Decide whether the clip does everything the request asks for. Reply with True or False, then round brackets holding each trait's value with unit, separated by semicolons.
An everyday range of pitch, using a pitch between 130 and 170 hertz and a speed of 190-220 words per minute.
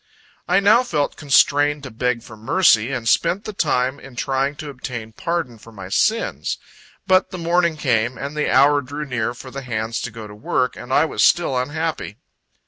True (4.7 semitones; 135 Hz; 195 wpm)